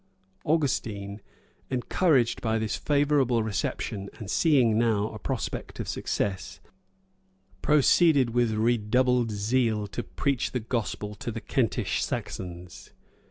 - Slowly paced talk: Yes, slow, 115 wpm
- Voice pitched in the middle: No, low, 115 Hz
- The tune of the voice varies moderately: Yes, average, 3.6 semitones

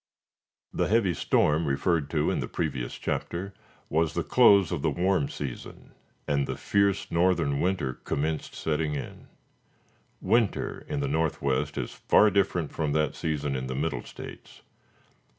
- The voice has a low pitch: Yes, very low, 80 Hz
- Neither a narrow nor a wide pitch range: Yes, average, 4.4 semitones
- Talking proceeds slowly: No, average, 150 wpm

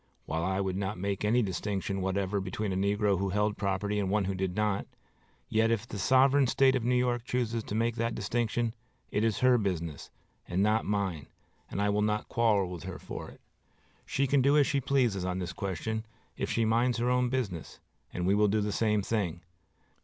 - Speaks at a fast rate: Yes, fast, 210 wpm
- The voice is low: Yes, low, 105 Hz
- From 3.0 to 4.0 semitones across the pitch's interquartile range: Yes, average, 3.4 semitones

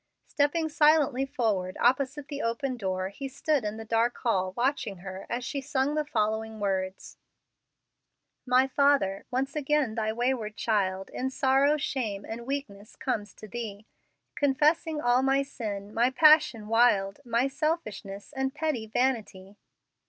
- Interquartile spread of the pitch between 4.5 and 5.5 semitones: Yes, average, 4.8 semitones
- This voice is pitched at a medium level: No, high, 245 Hz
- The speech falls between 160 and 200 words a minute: No, average, 145 wpm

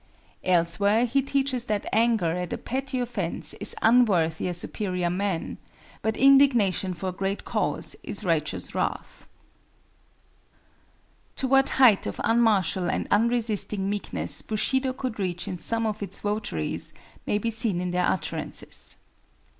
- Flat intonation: No, average, 4.6 semitones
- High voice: Yes, high, 210 Hz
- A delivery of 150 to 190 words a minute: No, average, 140 wpm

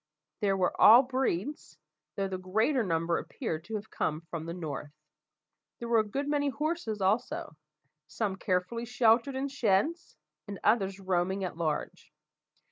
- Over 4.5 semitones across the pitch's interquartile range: Yes, average, 5.2 semitones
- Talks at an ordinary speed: Yes, average, 155 wpm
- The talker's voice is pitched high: Yes, high, 200 Hz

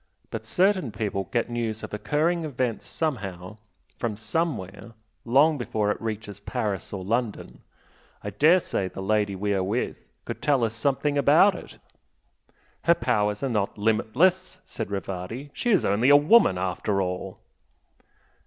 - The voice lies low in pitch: Yes, low, 110 Hz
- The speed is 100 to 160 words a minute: Yes, average, 150 wpm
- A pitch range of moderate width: No, wide, 6.0 semitones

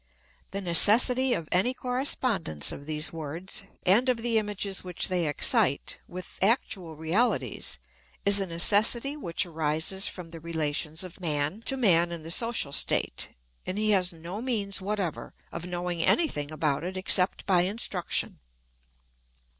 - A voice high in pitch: No, medium, 180 Hz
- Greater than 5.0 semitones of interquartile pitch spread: No, average, 4.4 semitones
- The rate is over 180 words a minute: No, average, 150 wpm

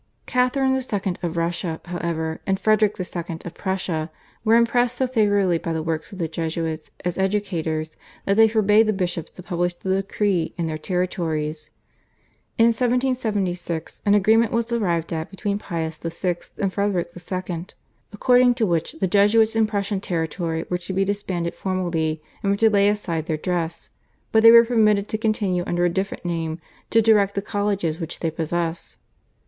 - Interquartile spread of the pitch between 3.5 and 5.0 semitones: Yes, average, 4.1 semitones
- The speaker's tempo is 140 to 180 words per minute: Yes, average, 170 wpm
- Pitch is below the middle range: No, high, 190 Hz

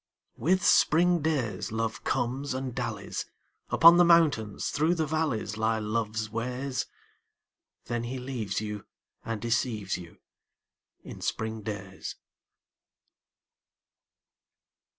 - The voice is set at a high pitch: No, low, 120 Hz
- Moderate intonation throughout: Yes, average, 4.8 semitones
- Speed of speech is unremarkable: No, slow, 105 wpm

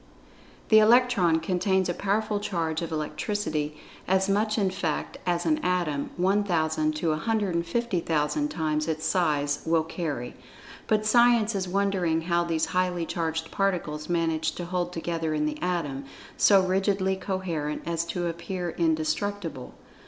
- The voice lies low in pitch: No, medium, 175 Hz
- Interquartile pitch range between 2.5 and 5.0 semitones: Yes, average, 3.6 semitones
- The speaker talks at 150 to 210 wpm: No, slow, 135 wpm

